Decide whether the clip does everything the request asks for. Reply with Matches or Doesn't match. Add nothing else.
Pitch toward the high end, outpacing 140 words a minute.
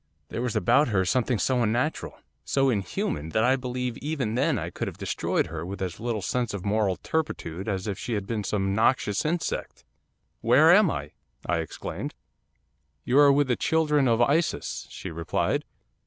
Doesn't match